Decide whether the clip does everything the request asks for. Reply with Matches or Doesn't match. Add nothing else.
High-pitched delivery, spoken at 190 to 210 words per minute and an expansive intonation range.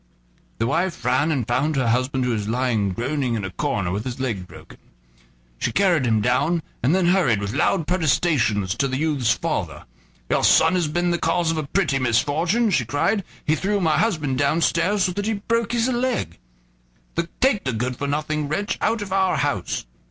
Doesn't match